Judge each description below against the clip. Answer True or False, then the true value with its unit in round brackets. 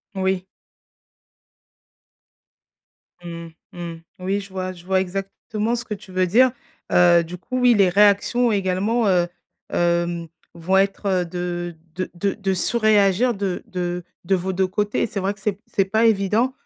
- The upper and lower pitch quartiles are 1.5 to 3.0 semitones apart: True (2.7 semitones)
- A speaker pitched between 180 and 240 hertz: True (190 Hz)